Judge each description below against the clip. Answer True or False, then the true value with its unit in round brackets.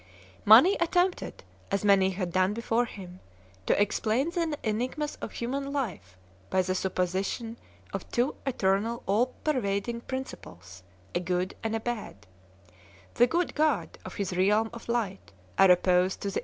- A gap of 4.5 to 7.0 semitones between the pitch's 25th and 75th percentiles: True (4.8 semitones)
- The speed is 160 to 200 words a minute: False (150 wpm)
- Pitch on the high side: True (215 Hz)